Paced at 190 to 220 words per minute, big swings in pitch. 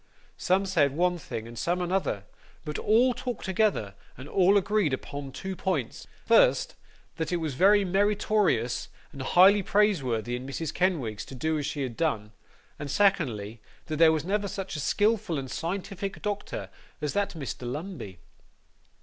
No: average, 160 wpm; wide, 6.5 semitones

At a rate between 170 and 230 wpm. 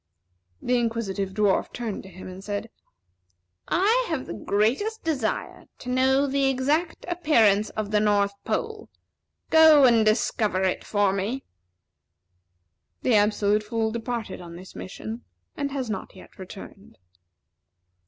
No: slow, 135 wpm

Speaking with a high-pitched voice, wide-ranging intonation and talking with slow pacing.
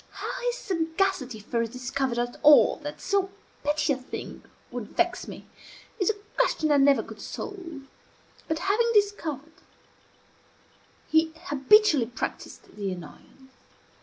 Yes: very high, 295 Hz; wide, 6.3 semitones; slow, 130 wpm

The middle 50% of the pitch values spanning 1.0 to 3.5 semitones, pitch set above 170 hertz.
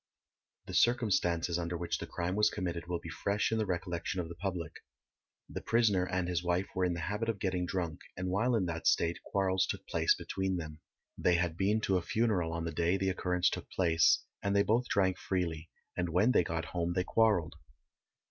No: narrow, 2.6 semitones; very low, 90 Hz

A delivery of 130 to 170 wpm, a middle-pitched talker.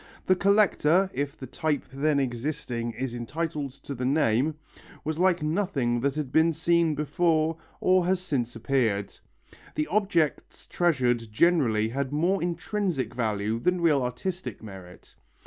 Yes: average, 140 wpm; medium, 150 Hz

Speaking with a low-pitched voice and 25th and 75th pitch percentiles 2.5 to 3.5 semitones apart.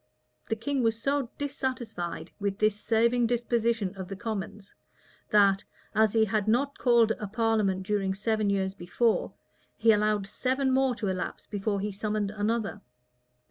No: high, 215 Hz; average, 2.8 semitones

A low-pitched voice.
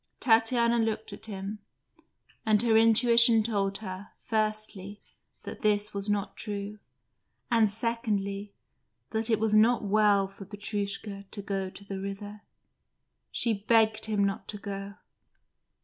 No: high, 210 Hz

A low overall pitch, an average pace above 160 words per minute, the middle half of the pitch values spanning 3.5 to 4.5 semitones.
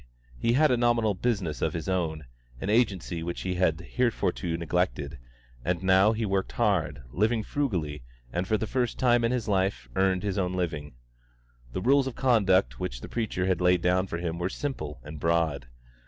No: very low, 95 Hz; average, 185 wpm; average, 5.1 semitones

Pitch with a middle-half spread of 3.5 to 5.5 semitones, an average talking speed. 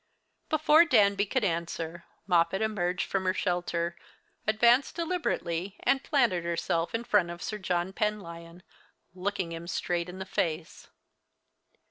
No: average, 3.9 semitones; slow, 130 wpm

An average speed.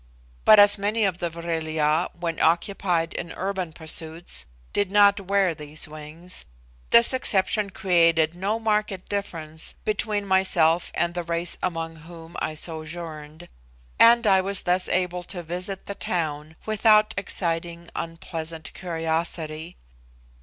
No: slow, 130 wpm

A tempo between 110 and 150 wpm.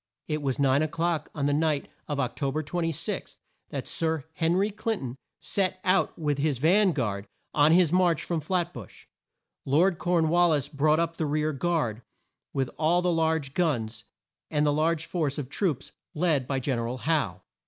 No: average, 190 wpm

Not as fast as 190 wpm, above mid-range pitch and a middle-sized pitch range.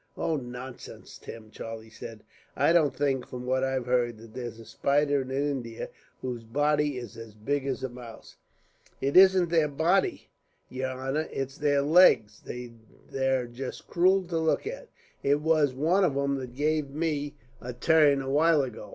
No: average, 170 wpm; low, 135 Hz; average, 3.5 semitones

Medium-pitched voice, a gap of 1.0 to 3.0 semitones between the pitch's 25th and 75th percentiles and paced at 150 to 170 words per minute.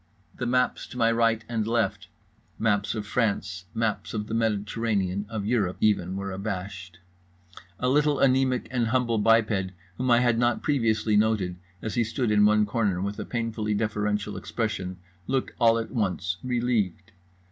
No: low, 110 Hz; narrow, 2.5 semitones; average, 160 wpm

